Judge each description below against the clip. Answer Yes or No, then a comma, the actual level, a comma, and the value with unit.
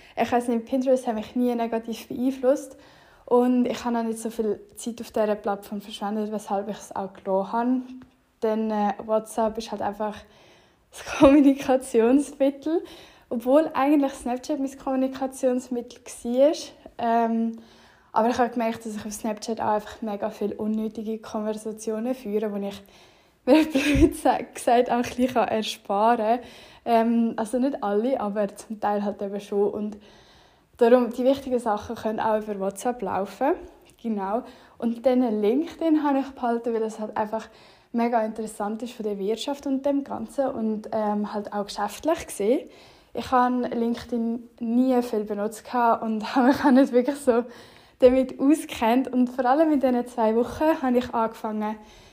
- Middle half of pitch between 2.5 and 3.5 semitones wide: Yes, average, 3.1 semitones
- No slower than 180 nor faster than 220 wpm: No, average, 155 wpm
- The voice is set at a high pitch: Yes, high, 235 Hz